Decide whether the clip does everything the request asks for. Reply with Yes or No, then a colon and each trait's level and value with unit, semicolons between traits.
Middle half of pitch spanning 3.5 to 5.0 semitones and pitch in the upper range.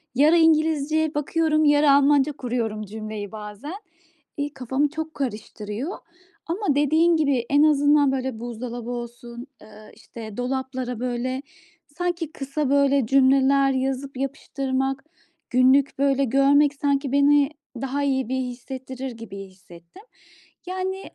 No: average, 2.9 semitones; very high, 270 Hz